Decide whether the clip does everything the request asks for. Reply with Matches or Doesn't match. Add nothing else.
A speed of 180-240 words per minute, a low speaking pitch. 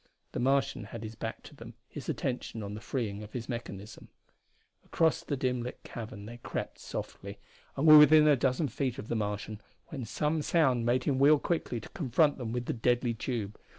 Matches